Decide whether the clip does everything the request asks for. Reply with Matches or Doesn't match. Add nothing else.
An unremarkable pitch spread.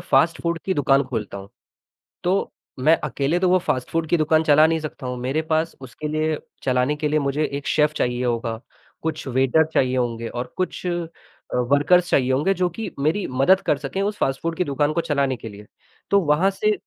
Matches